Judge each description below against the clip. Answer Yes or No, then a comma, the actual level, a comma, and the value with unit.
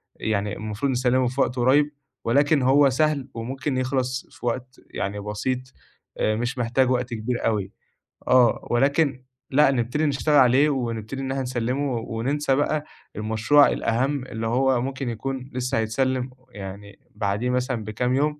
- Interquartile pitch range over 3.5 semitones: No, average, 3.0 semitones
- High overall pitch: No, low, 125 Hz